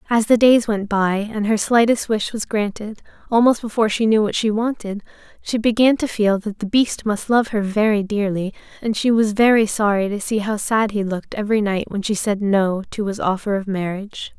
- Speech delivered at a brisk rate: Yes, fast, 215 wpm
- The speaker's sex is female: Yes, female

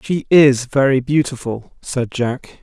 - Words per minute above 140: No, slow, 135 wpm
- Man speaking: Yes, male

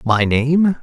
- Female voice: No, male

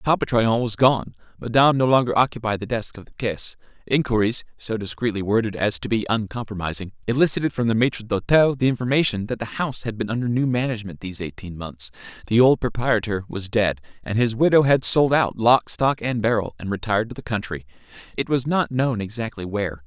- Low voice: Yes, low, 115 Hz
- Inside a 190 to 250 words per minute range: Yes, average, 195 wpm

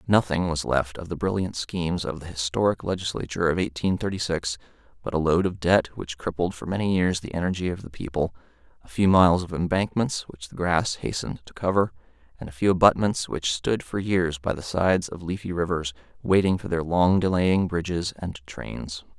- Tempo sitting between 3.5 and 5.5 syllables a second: Yes, 5.4 syllables/s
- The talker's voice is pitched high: No, very low, 90 Hz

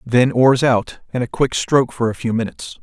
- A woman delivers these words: No, male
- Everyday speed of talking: No, fast, 235 wpm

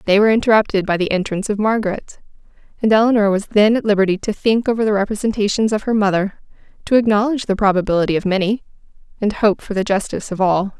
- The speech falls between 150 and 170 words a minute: No, average, 195 wpm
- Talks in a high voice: Yes, high, 205 Hz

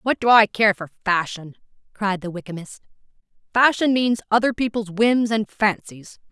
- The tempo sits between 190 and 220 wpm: No, average, 150 wpm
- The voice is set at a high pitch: Yes, high, 210 Hz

